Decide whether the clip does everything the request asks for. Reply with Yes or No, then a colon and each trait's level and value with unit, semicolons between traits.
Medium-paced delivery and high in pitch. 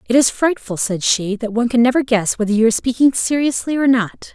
No: fast, 235 wpm; high, 240 Hz